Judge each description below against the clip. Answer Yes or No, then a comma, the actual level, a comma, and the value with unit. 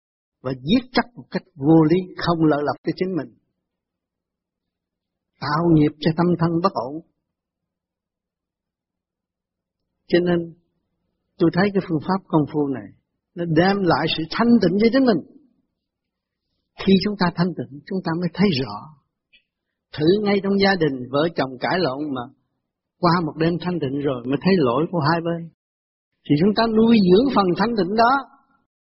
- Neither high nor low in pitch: Yes, medium, 170 Hz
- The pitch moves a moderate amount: Yes, average, 4.8 semitones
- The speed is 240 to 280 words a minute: No, slow, 165 wpm